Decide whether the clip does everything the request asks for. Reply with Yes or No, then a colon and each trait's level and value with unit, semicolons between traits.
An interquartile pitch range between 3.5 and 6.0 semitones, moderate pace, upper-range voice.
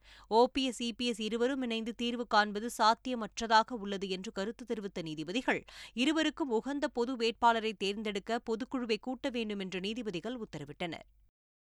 No: average, 2.9 semitones; average, 120 wpm; high, 230 Hz